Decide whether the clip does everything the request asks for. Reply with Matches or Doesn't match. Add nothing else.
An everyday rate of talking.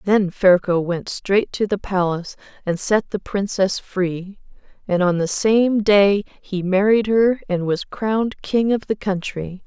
Matches